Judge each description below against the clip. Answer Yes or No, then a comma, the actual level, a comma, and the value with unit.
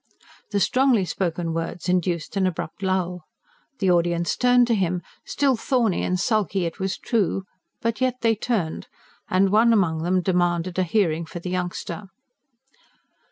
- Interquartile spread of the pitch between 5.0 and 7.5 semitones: No, average, 3.9 semitones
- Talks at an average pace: Yes, average, 155 wpm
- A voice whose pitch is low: No, medium, 185 Hz